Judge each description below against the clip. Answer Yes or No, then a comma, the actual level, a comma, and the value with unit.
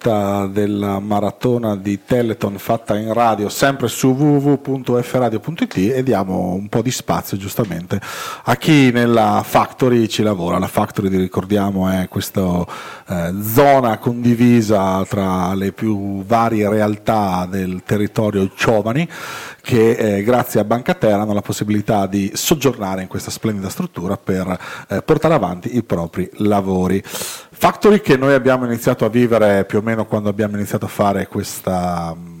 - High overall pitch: No, low, 105 Hz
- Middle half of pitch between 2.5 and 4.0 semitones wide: Yes, average, 3.6 semitones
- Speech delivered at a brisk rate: No, average, 145 wpm